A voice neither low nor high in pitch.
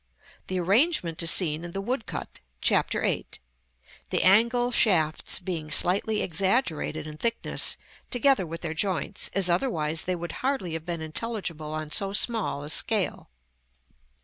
Yes: medium, 180 Hz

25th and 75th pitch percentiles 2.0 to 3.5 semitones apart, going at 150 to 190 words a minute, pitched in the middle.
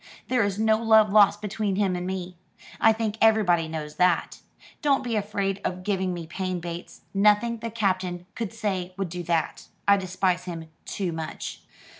No: average, 3.2 semitones; average, 175 wpm; high, 195 Hz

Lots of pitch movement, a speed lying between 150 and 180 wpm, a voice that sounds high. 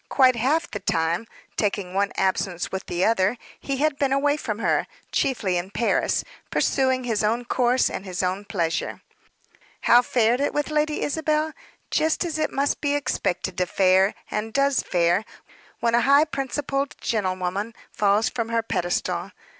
Yes: wide, 6.4 semitones; average, 160 wpm; high, 230 Hz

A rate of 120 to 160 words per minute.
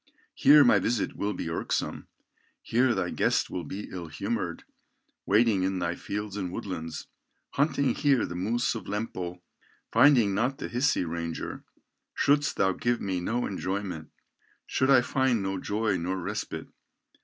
Yes: average, 150 wpm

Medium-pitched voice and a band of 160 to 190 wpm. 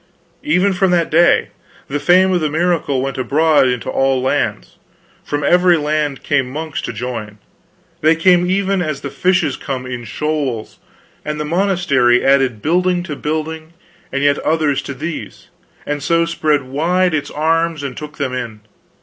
Yes: medium, 150 Hz; average, 165 wpm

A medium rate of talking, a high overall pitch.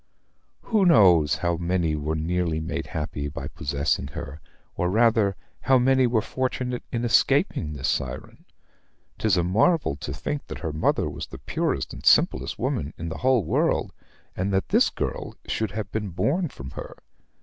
No: average, 170 wpm; very low, 90 Hz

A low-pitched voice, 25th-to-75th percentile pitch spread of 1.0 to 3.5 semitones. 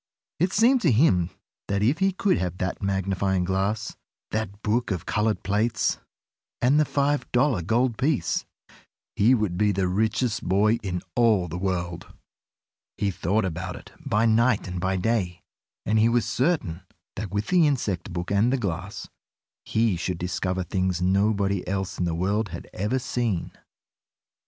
No: low, 105 Hz; average, 4.2 semitones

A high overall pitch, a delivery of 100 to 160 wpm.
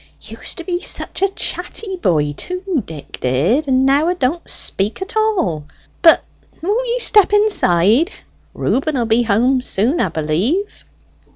Yes: very high, 275 Hz; average, 155 wpm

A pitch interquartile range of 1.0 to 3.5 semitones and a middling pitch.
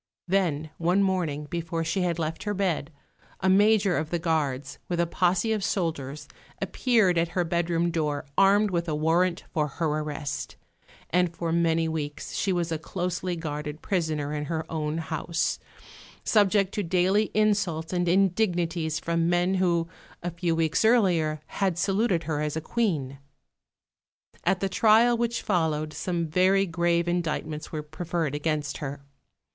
Yes: average, 3.0 semitones; medium, 170 Hz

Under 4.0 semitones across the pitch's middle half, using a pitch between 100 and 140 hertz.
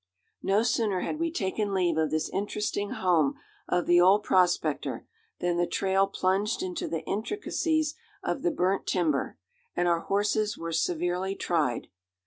No: average, 3.3 semitones; high, 190 Hz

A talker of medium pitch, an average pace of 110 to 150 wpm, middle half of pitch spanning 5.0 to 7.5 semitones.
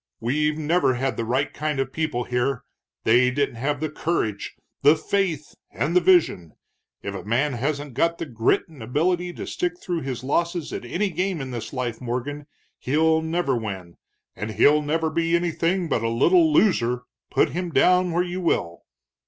No: medium, 145 Hz; average, 180 wpm; wide, 5.4 semitones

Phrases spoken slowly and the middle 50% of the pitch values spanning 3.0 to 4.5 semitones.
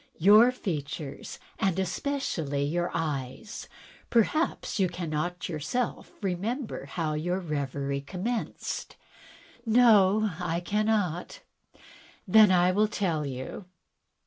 No: slow, 100 wpm; wide, 5.6 semitones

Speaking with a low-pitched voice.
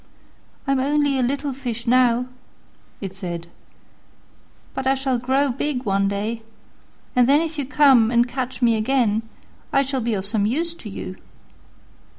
No: very high, 250 Hz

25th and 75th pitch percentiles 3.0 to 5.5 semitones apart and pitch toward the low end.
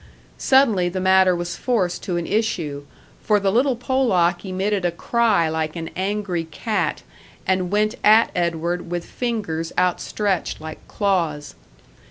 No: average, 3.6 semitones; medium, 185 Hz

